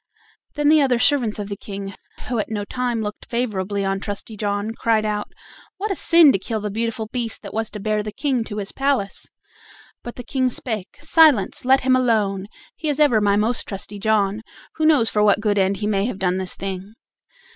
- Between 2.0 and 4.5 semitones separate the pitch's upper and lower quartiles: Yes, average, 3.7 semitones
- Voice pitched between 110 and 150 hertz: No, high, 215 Hz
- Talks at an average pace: No, fast, 210 wpm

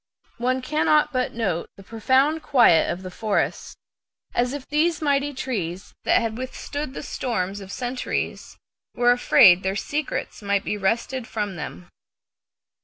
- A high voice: Yes, high, 240 Hz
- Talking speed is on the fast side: No, average, 145 wpm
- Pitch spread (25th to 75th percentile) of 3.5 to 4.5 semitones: No, wide, 5.6 semitones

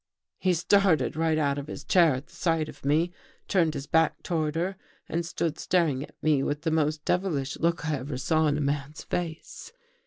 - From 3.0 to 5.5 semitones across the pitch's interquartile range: No, narrow, 2.6 semitones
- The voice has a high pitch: No, medium, 155 Hz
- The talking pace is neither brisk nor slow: No, fast, 210 wpm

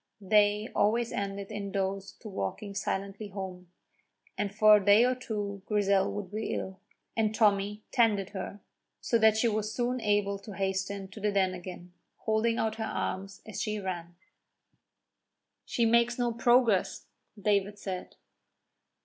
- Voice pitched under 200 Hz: No, high, 205 Hz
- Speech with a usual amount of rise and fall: No, narrow, 2.0 semitones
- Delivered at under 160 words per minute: Yes, average, 150 wpm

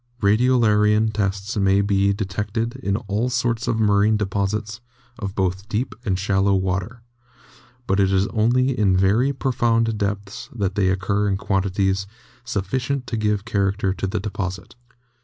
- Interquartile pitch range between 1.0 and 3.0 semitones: Yes, narrow, 2.6 semitones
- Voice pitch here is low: Yes, low, 100 Hz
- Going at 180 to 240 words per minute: No, average, 150 wpm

